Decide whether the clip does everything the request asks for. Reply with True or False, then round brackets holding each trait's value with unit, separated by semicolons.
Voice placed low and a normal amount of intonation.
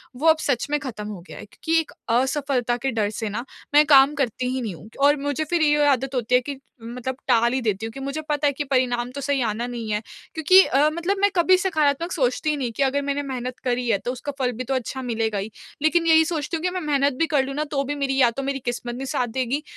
False (270 Hz; 3.3 semitones)